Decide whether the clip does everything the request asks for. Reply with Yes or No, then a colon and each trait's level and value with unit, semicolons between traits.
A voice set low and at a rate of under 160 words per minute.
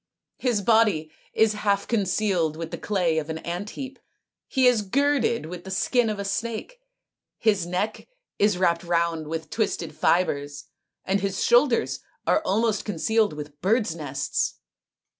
No: high, 195 Hz; average, 150 wpm